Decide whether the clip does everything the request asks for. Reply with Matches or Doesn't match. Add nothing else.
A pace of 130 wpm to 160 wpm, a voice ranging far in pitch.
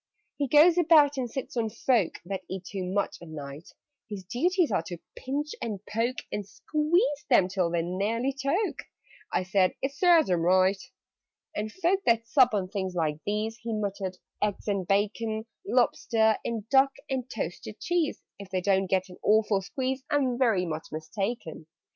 Doesn't match